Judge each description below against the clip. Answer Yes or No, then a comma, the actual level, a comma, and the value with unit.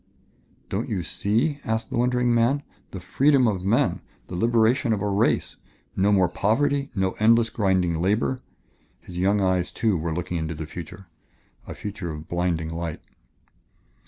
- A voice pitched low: Yes, low, 100 Hz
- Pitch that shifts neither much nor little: Yes, average, 4.7 semitones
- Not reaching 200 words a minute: Yes, average, 160 wpm